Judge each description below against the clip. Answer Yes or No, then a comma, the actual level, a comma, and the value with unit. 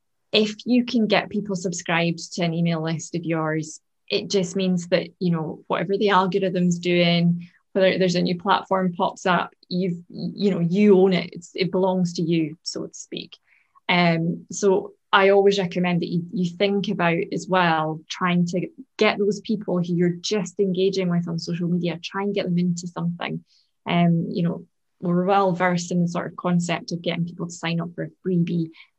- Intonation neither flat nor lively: No, narrow, 2.1 semitones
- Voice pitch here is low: No, medium, 180 Hz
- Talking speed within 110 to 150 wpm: No, average, 195 wpm